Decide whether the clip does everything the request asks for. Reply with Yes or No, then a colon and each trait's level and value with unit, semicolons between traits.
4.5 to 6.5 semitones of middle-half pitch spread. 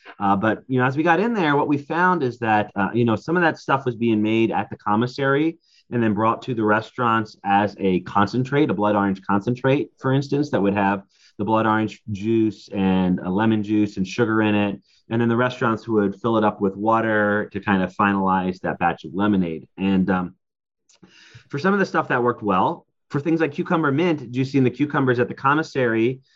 Yes: average, 4.8 semitones